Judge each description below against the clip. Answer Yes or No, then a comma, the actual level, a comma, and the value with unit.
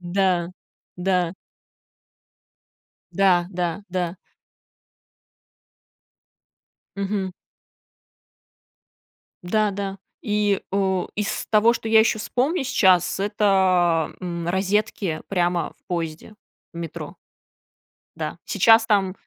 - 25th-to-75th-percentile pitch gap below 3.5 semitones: Yes, average, 2.9 semitones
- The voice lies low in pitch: No, high, 190 Hz